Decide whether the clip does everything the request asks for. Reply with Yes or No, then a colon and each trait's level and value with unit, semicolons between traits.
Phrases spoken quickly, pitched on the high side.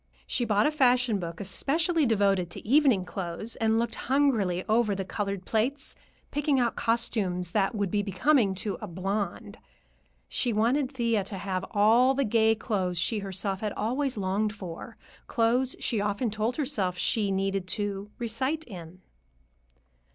No: average, 155 wpm; high, 215 Hz